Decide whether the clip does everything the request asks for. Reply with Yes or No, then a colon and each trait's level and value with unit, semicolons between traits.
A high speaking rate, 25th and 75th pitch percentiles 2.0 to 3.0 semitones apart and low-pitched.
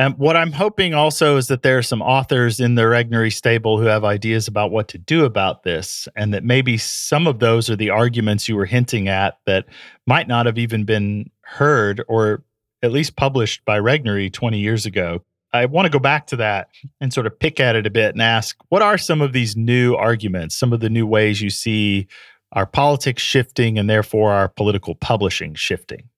No: fast, 215 wpm; average, 3.8 semitones; low, 115 Hz